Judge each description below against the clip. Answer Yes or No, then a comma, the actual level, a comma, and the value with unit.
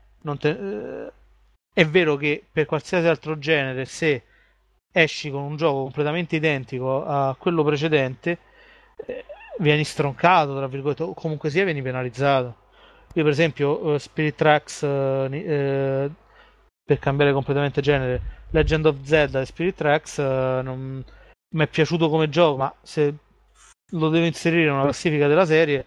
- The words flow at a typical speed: Yes, average, 145 wpm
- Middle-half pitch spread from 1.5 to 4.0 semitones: Yes, average, 2.8 semitones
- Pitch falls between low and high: Yes, medium, 150 Hz